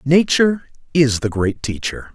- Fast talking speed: No, average, 140 wpm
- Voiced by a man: Yes, male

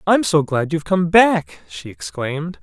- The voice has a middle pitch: Yes, medium, 160 Hz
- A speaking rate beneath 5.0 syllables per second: Yes, 4.5 syllables/s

